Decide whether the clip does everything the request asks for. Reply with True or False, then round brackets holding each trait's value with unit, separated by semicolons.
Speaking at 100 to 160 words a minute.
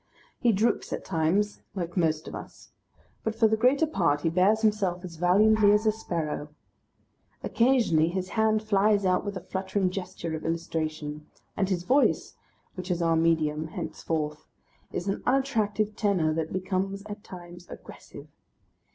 True (155 wpm)